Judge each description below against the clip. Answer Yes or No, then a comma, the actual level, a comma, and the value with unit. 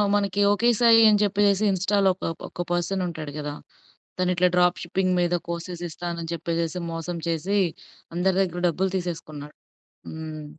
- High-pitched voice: No, medium, 175 Hz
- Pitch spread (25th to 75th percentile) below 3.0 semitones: Yes, narrow, 2.4 semitones